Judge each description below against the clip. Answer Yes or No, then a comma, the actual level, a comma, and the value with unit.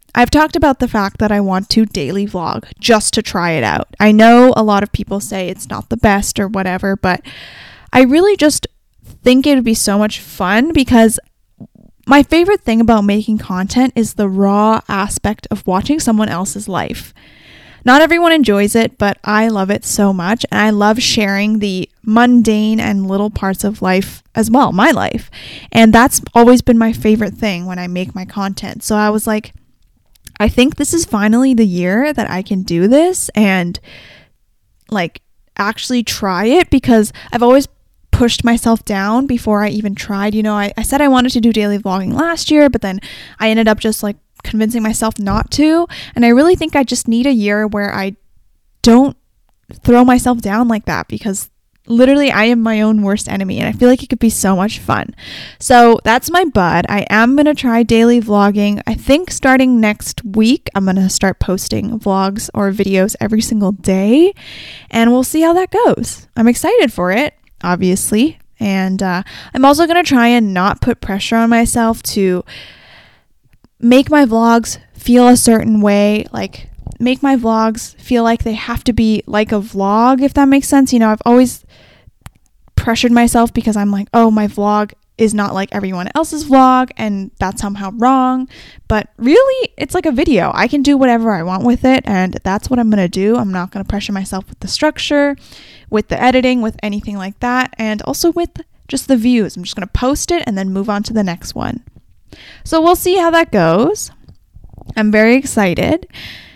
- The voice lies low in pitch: No, high, 220 Hz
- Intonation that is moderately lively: Yes, average, 3.7 semitones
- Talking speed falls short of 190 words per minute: No, average, 195 wpm